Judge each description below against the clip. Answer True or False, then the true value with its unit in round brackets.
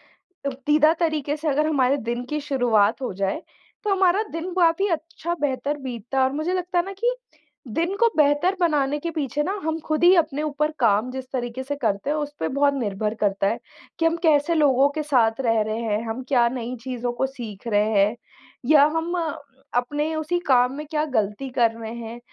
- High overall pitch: True (280 Hz)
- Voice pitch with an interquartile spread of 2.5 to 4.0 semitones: False (4.7 semitones)